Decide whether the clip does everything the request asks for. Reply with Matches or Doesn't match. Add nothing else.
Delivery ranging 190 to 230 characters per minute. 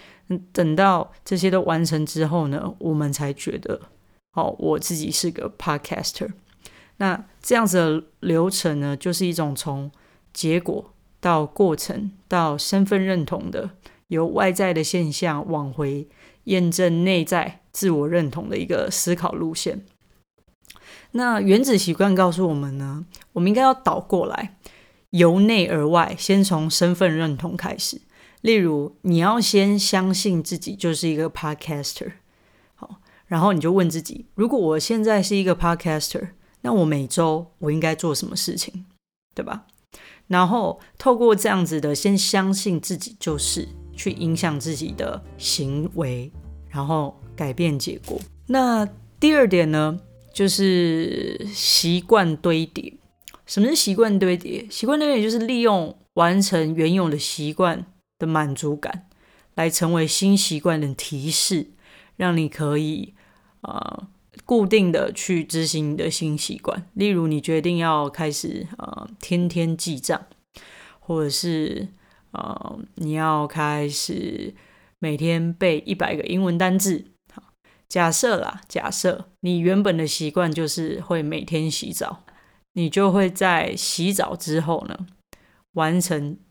Matches